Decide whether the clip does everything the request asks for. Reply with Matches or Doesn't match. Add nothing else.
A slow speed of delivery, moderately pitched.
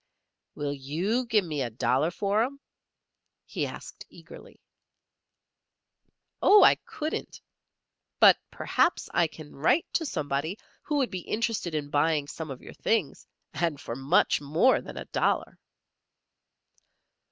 Matches